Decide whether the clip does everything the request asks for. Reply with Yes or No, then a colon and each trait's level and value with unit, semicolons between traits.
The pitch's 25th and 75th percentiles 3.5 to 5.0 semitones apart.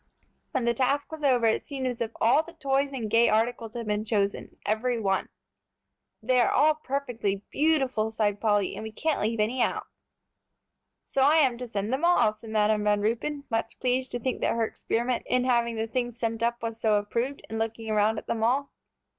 No: average, 3.1 semitones